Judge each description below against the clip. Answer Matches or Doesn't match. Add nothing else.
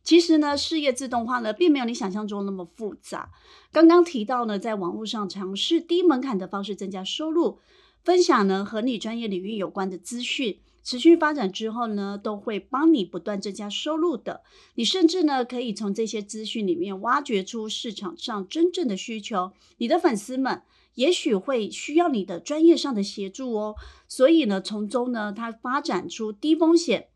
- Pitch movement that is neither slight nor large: Doesn't match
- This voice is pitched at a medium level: Doesn't match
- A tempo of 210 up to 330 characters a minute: Matches